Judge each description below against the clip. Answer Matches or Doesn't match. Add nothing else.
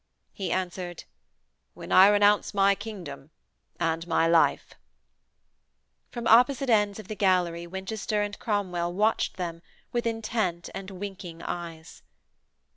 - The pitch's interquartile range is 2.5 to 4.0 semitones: Matches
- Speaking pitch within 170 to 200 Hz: Matches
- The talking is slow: Matches